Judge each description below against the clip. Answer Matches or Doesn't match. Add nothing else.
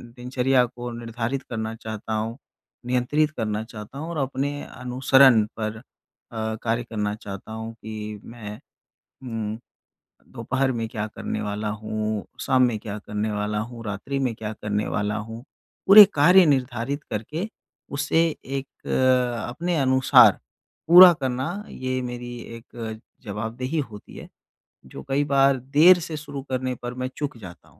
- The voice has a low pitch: Matches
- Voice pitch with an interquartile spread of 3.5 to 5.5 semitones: Matches